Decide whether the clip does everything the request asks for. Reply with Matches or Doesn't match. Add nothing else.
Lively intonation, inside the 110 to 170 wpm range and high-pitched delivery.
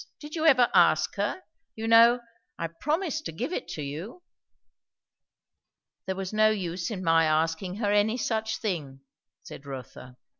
Matches